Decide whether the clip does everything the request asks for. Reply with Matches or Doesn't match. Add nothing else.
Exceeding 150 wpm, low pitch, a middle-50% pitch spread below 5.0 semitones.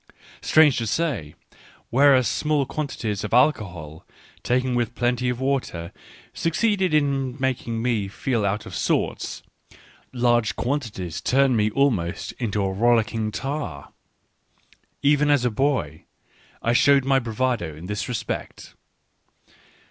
Doesn't match